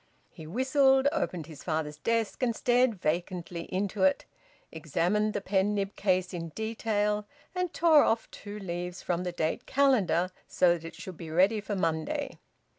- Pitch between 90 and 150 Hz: No, high, 190 Hz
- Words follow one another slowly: No, average, 165 wpm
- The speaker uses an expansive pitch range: No, average, 4.5 semitones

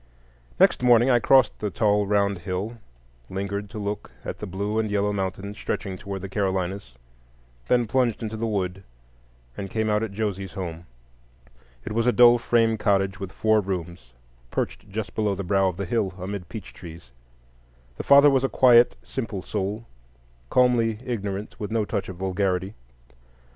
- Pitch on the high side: No, low, 100 Hz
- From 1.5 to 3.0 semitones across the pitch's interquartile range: Yes, average, 2.7 semitones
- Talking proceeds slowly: No, average, 170 wpm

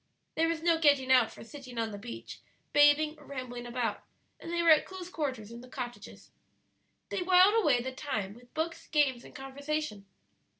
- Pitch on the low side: No, very high, 275 Hz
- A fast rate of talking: No, average, 185 wpm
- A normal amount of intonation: Yes, average, 4.6 semitones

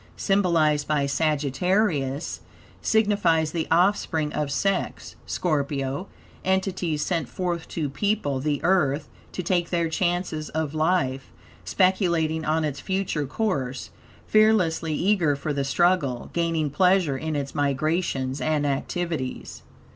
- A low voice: No, medium, 160 Hz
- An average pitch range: Yes, average, 4.1 semitones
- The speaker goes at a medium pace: No, slow, 115 wpm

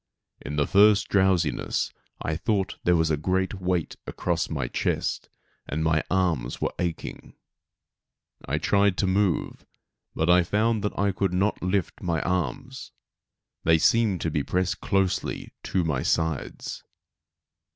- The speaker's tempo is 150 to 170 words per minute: No, average, 140 wpm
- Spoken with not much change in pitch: No, average, 3.4 semitones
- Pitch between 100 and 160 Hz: No, very low, 90 Hz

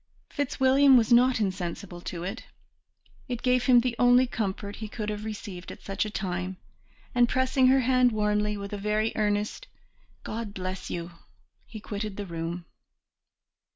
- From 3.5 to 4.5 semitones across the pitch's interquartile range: Yes, average, 4.0 semitones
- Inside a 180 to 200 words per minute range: No, average, 155 wpm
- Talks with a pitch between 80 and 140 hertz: No, high, 210 Hz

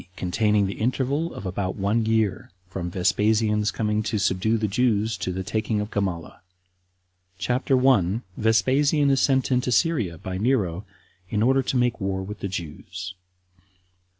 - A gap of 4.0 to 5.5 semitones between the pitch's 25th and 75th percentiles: Yes, average, 4.5 semitones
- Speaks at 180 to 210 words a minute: No, average, 150 wpm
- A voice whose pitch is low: Yes, low, 105 Hz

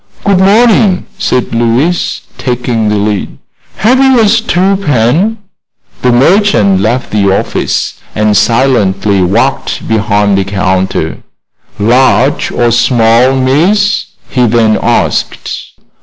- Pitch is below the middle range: Yes, low, 120 Hz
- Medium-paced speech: No, slow, 110 wpm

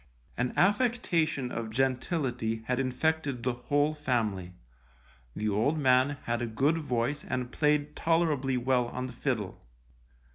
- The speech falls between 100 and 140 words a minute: Yes, slow, 135 wpm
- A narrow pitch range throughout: No, average, 3.7 semitones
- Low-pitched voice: Yes, low, 130 Hz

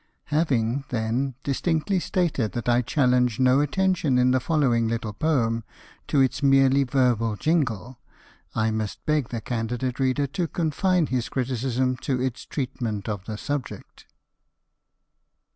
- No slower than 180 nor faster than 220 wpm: No, slow, 135 wpm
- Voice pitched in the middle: No, low, 130 Hz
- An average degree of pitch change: Yes, average, 3.6 semitones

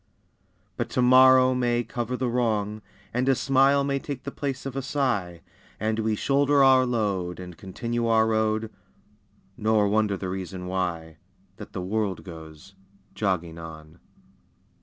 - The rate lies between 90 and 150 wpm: Yes, average, 140 wpm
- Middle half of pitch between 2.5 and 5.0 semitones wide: No, wide, 5.5 semitones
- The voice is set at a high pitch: No, low, 110 Hz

